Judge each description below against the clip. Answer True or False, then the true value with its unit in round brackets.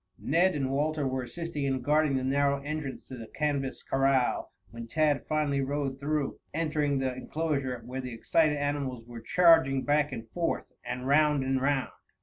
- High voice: False (140 Hz)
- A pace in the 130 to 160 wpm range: False (170 wpm)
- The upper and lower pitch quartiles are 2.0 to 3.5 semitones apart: True (2.4 semitones)